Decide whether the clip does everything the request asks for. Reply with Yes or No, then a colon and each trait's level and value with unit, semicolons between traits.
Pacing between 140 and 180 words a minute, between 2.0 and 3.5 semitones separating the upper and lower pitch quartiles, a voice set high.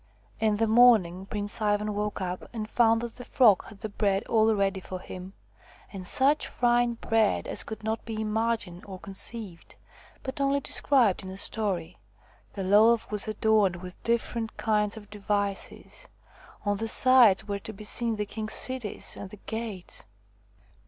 Yes: average, 170 wpm; narrow, 2.5 semitones; high, 215 Hz